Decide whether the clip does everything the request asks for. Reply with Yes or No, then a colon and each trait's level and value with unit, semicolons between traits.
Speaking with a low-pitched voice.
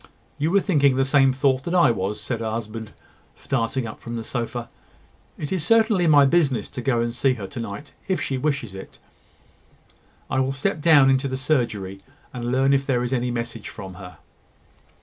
Yes: low, 130 Hz